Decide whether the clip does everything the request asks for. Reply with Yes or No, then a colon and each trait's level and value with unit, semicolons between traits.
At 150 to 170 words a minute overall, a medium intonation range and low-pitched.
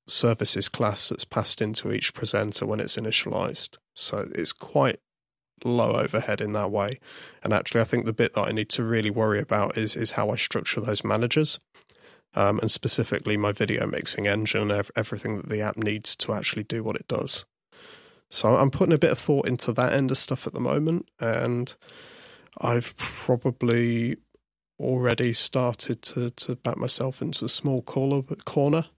No: average, 180 wpm; average, 3.1 semitones; low, 120 Hz